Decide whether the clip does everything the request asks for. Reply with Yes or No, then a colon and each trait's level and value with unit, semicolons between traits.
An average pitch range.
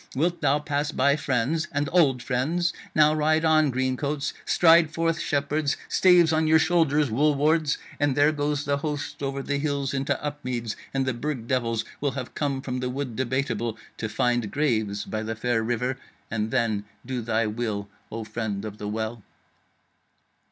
Yes: average, 4.2 semitones